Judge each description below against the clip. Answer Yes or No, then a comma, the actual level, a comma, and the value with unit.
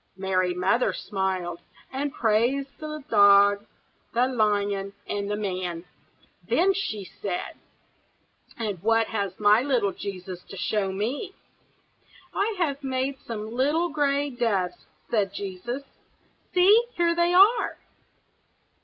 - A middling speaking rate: No, slow, 120 wpm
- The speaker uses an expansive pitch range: Yes, wide, 6.0 semitones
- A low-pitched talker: No, high, 220 Hz